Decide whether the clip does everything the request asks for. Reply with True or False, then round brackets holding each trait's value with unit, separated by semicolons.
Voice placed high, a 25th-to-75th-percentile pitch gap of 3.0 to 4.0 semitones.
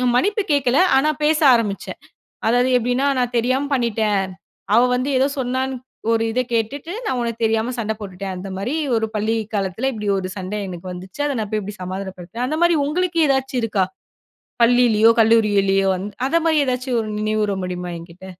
False (225 Hz; 4.6 semitones)